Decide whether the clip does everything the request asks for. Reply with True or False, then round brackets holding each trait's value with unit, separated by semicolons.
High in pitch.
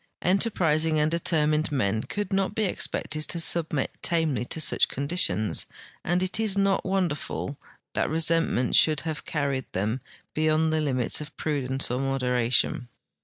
False (155 Hz)